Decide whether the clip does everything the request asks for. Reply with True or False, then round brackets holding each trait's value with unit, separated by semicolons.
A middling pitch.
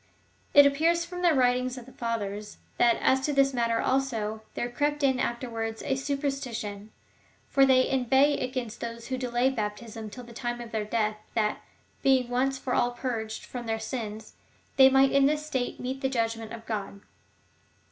False (245 Hz)